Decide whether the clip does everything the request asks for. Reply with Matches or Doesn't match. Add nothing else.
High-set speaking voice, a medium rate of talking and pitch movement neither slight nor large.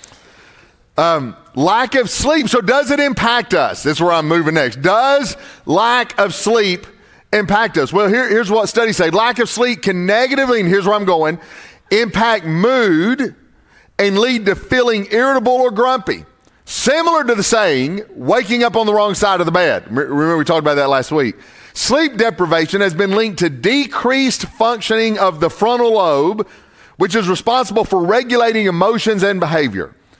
Matches